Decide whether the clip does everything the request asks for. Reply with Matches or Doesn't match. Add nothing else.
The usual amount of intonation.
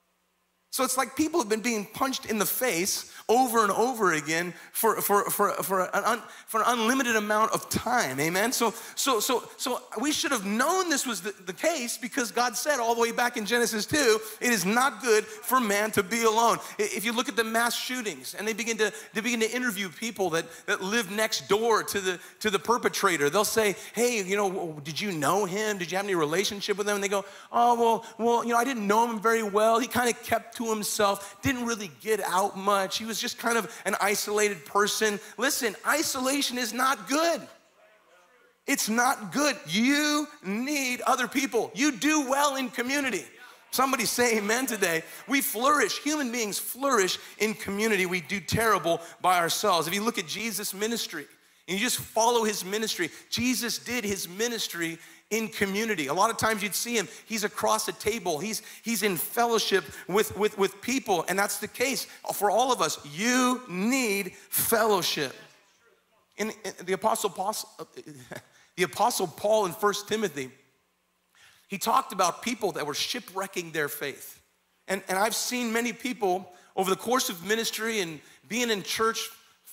Matches